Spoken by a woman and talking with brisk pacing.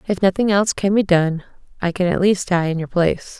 Yes: female; fast, 250 wpm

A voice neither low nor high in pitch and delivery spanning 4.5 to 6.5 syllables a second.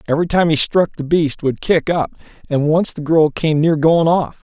Yes: medium, 160 Hz; 5.0 syllables/s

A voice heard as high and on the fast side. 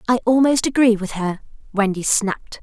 No: high, 220 Hz; average, 160 wpm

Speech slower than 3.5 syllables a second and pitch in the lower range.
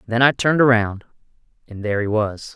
No: 6.2 syllables/s; low, 115 Hz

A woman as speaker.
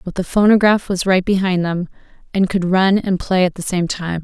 Yes: female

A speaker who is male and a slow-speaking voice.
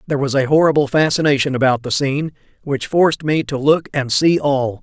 No: male; average, 200 wpm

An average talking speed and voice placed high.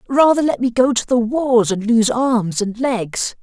No: fast, 210 wpm; high, 240 Hz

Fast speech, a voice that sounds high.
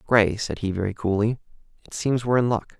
No: fast, 215 wpm; low, 110 Hz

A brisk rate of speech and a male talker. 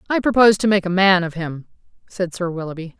No: fast, 220 wpm; female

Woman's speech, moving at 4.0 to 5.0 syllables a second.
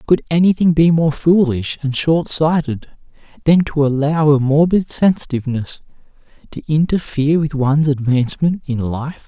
No: male; 4.9 syllables/s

